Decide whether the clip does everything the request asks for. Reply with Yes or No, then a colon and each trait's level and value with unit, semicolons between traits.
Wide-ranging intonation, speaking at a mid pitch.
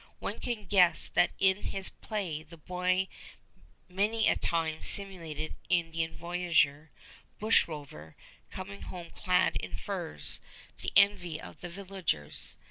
No: average, 3.4 semitones; medium, 175 Hz